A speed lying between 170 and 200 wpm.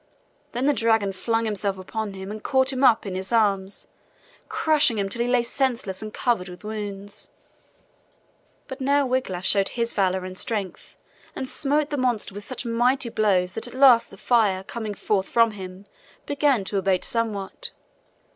Yes: average, 175 wpm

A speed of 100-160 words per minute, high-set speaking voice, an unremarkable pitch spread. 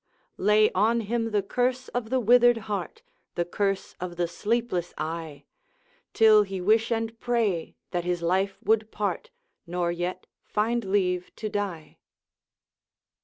Yes: average, 140 wpm; high, 205 Hz; average, 4.1 semitones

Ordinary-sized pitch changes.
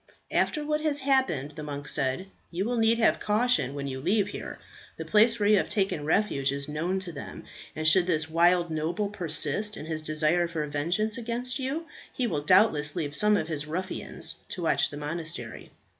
No: wide, 5.9 semitones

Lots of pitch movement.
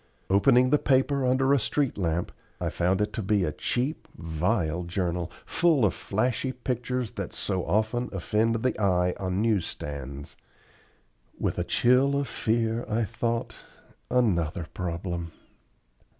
Yes: wide, 5.9 semitones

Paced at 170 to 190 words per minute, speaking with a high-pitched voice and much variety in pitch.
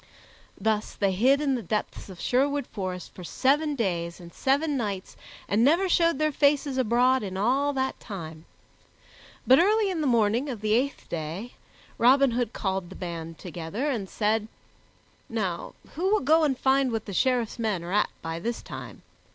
Yes: average, 175 wpm; high, 235 Hz; wide, 6.3 semitones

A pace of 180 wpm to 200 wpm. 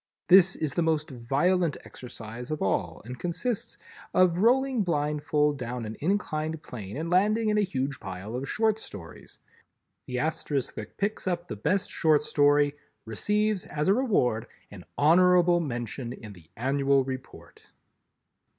No: average, 150 wpm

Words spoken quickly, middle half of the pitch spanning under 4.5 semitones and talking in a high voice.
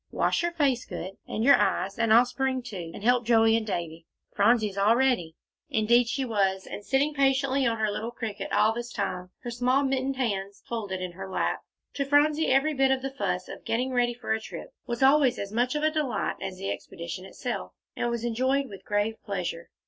No: fast, 210 wpm; average, 4.8 semitones; high, 235 Hz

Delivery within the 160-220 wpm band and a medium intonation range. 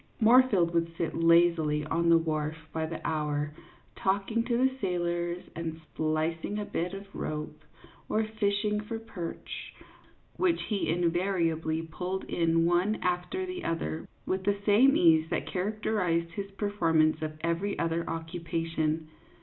No: average, 140 wpm; average, 3.8 semitones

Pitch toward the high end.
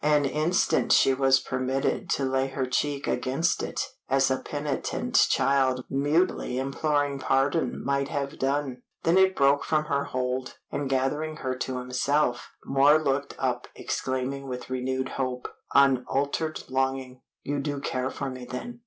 No: low, 135 Hz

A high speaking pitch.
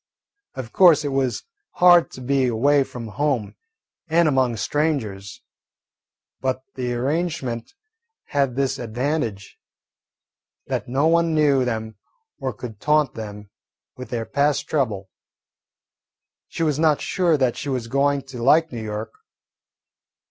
No: low, 135 Hz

